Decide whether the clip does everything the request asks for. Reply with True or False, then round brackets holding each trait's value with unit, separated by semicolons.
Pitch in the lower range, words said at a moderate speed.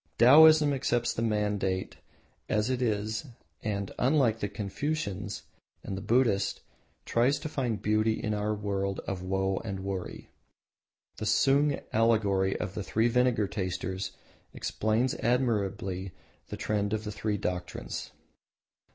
False (105 Hz; 130 wpm)